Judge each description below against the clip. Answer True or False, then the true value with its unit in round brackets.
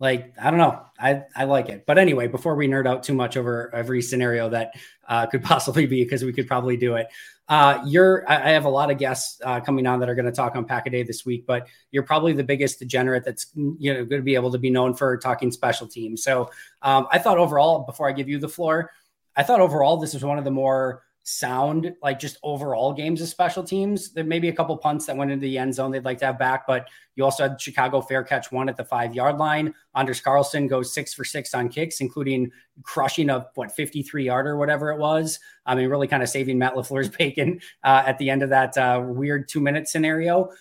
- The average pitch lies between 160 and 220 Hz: False (135 Hz)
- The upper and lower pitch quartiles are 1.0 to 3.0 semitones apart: True (2.7 semitones)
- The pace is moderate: False (250 wpm)